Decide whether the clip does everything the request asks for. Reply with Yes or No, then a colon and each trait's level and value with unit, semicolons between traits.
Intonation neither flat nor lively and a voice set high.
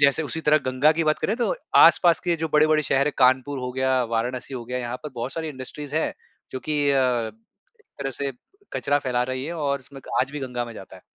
No: average, 3.2 semitones; low, 135 Hz